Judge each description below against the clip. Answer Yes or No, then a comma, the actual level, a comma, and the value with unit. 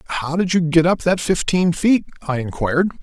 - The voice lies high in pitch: No, medium, 165 Hz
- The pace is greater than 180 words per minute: Yes, average, 200 wpm